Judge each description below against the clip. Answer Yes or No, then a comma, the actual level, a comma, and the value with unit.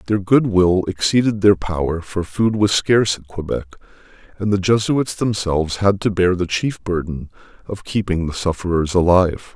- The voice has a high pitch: No, very low, 95 Hz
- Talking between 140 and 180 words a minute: Yes, average, 170 wpm